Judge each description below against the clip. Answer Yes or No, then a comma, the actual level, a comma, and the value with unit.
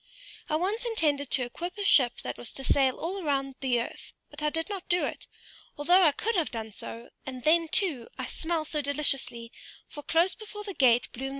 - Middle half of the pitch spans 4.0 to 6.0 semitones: Yes, average, 5.1 semitones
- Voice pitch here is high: Yes, very high, 300 Hz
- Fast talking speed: Yes, fast, 230 wpm